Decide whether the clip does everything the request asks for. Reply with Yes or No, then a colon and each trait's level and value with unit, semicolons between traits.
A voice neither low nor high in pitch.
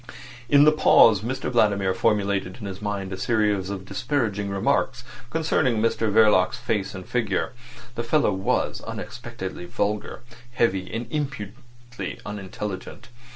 No: low, 105 Hz